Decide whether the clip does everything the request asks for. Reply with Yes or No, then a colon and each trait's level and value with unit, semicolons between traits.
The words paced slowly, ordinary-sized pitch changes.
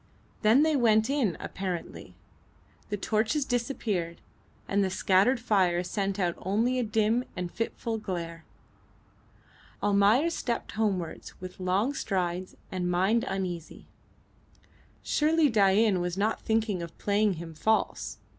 Yes: slow, 125 wpm; average, 3.8 semitones